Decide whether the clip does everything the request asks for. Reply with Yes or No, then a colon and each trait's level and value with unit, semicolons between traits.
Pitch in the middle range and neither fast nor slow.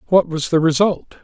Yes: medium, 170 Hz; average, 195 wpm